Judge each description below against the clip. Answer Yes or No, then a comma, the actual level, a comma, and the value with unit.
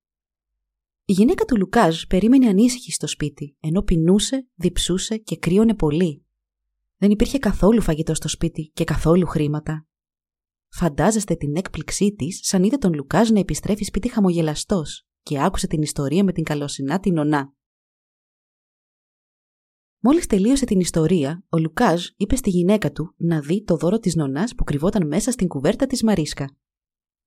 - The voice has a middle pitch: Yes, medium, 170 Hz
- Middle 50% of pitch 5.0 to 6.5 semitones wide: Yes, average, 5.3 semitones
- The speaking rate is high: No, average, 145 wpm